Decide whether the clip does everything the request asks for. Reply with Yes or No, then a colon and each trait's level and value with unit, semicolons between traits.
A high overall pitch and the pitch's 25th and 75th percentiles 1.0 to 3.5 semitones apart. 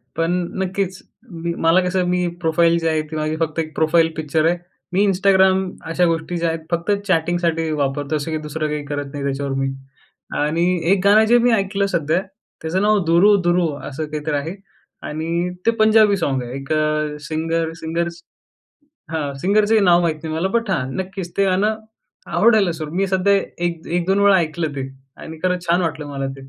No: medium, 170 Hz; average, 3.2 semitones